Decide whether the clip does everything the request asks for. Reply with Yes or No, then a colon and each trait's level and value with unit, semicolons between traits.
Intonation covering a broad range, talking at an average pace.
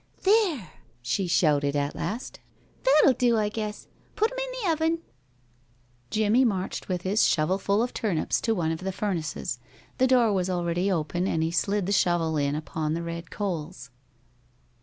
Yes: wide, 5.8 semitones; average, 165 wpm